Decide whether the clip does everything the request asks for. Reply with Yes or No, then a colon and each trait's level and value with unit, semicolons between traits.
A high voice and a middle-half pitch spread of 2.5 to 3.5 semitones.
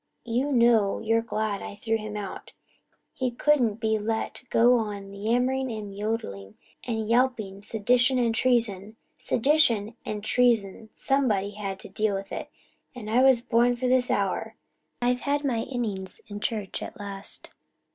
Yes: high, 225 Hz; average, 3.2 semitones